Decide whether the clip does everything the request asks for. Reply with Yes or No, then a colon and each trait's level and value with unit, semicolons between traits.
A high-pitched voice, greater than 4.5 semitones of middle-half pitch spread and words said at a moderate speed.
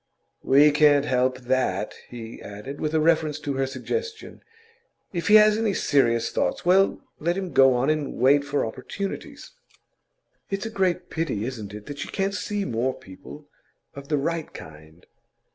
No: medium, 145 Hz; wide, 5.4 semitones; average, 160 wpm